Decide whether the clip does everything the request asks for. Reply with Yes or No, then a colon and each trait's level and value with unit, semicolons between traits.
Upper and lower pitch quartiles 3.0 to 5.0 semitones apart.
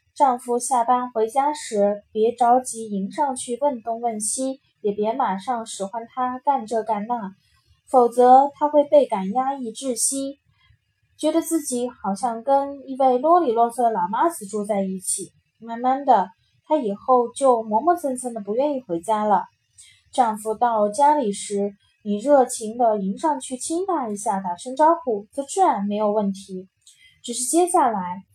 Yes: average, 4.7 semitones